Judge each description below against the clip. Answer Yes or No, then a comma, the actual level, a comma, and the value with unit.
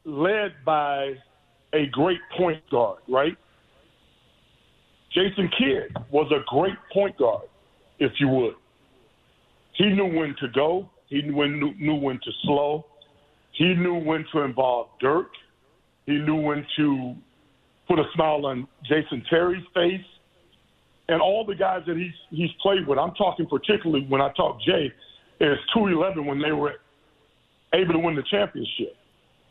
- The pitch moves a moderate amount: Yes, average, 4.0 semitones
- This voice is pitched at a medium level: Yes, medium, 155 Hz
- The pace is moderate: Yes, average, 150 wpm